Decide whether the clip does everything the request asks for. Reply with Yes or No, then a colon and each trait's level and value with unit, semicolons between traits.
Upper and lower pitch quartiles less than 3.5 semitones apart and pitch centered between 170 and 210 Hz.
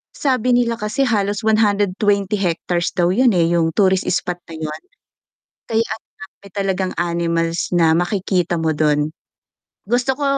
No: average, 4.0 semitones; high, 190 Hz